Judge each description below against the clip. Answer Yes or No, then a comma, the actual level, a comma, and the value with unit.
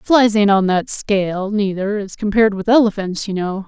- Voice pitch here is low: No, high, 205 Hz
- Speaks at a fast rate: No, average, 195 wpm